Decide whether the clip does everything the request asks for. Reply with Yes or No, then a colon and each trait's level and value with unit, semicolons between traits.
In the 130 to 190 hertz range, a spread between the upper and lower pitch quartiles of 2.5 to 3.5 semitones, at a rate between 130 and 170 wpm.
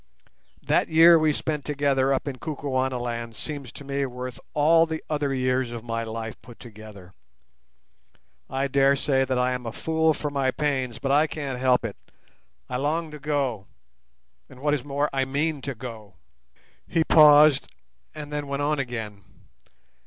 Yes: low, 135 Hz; average, 2.9 semitones; average, 165 wpm